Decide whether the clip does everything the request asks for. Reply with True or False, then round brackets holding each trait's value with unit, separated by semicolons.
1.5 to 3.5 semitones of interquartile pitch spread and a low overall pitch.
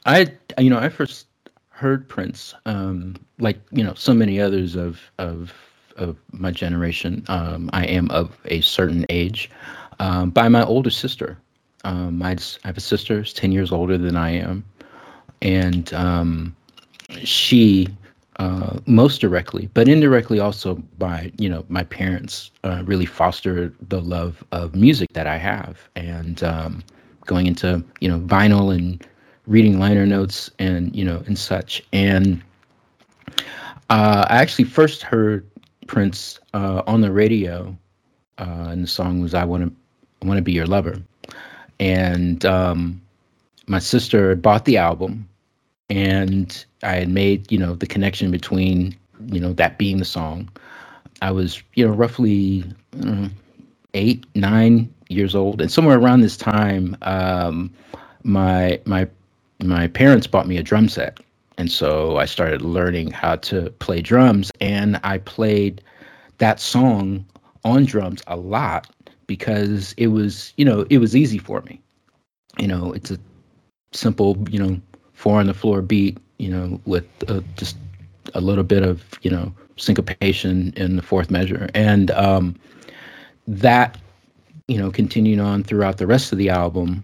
True (2.9 semitones; 95 Hz)